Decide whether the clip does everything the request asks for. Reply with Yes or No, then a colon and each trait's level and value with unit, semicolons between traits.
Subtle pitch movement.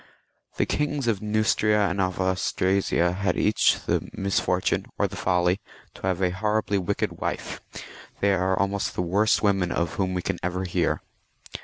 Yes: narrow, 2.0 semitones